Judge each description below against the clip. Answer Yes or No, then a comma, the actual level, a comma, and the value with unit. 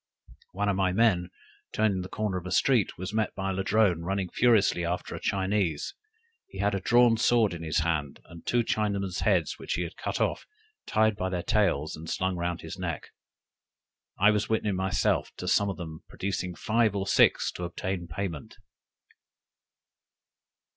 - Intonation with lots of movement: No, average, 3.2 semitones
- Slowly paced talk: No, average, 175 wpm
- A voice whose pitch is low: Yes, very low, 95 Hz